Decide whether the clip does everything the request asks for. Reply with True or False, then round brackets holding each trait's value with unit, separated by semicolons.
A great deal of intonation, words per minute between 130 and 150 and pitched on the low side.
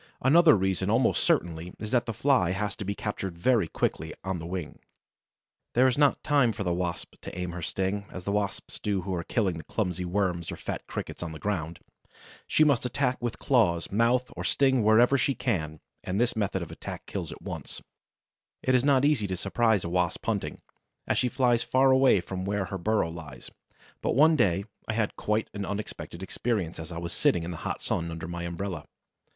False (5.7 semitones; 205 wpm; 100 Hz)